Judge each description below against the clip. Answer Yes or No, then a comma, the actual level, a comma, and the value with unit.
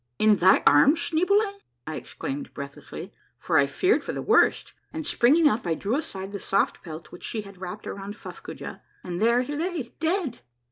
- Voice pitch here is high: Yes, high, 230 Hz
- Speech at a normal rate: Yes, average, 195 wpm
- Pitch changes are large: Yes, wide, 8.9 semitones